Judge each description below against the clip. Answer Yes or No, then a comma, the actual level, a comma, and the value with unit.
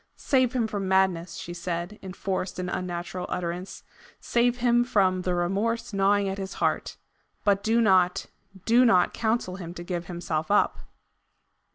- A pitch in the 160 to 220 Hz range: Yes, high, 190 Hz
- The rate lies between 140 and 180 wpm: Yes, average, 160 wpm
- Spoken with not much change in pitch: No, average, 3.7 semitones